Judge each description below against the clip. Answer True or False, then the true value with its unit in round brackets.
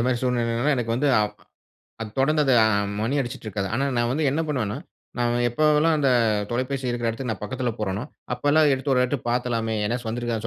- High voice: False (125 Hz)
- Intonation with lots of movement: False (2.9 semitones)